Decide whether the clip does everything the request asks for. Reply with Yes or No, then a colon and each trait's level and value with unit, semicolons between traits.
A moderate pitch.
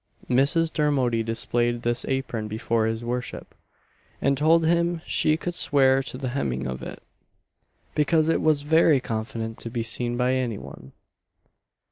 No: low, 130 Hz